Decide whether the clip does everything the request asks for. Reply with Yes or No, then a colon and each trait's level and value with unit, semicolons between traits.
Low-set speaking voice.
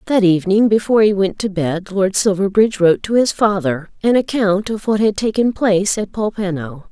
No: high, 200 Hz